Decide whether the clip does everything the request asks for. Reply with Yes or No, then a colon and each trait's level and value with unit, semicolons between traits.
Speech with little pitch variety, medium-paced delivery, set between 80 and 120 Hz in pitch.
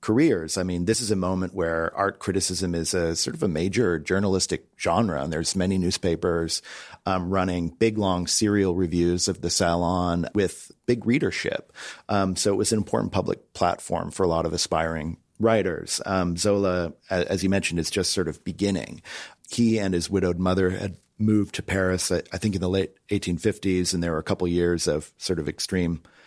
Yes: narrow, 2.3 semitones; average, 190 wpm; very low, 90 Hz